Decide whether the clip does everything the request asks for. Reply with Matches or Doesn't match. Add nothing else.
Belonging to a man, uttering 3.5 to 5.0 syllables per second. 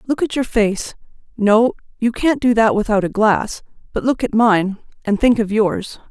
Doesn't match